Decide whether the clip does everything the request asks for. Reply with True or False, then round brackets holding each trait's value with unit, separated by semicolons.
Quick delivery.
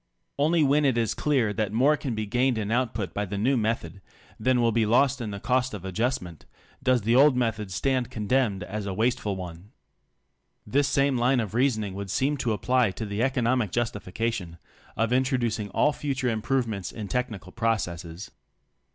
False (180 wpm)